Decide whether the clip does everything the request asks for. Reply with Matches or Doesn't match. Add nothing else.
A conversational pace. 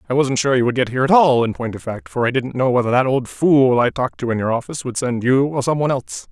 Doesn't match